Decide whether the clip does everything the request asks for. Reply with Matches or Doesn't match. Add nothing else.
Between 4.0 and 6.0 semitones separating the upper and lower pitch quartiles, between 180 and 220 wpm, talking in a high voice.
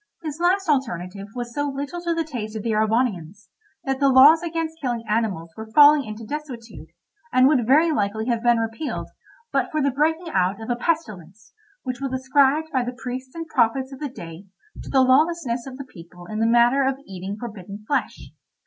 Matches